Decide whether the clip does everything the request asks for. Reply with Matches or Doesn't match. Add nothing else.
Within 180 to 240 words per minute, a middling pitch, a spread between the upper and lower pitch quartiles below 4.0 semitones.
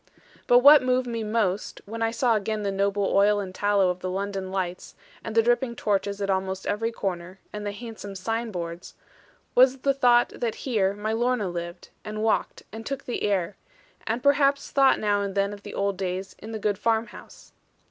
Doesn't match